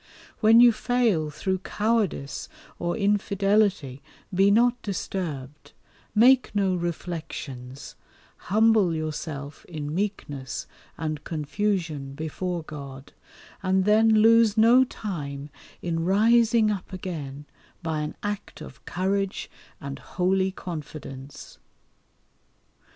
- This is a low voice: No, medium, 185 Hz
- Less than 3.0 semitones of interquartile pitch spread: No, wide, 5.6 semitones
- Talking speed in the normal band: No, slow, 100 wpm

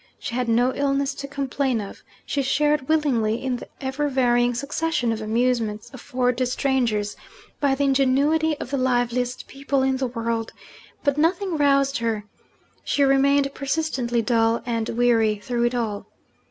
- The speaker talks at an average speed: Yes, average, 155 wpm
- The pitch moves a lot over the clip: No, average, 2.9 semitones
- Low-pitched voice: No, very high, 255 Hz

